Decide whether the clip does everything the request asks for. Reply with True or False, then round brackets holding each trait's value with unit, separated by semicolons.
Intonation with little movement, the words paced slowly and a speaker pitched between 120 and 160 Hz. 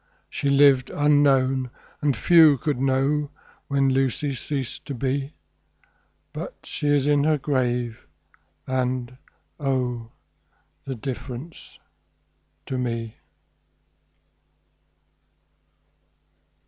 True (2.2 semitones; 90 wpm; 135 Hz)